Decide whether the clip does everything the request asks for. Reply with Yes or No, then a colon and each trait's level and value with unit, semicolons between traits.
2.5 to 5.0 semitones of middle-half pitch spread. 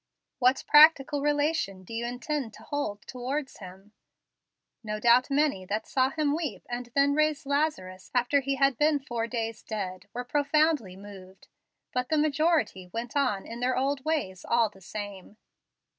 No: wide, 5.4 semitones